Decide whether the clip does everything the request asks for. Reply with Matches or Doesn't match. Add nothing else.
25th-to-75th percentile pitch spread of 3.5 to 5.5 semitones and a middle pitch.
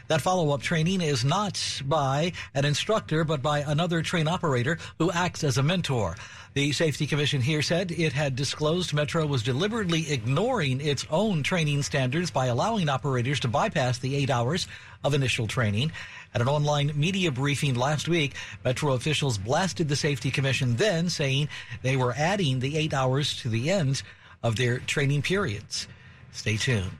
Matches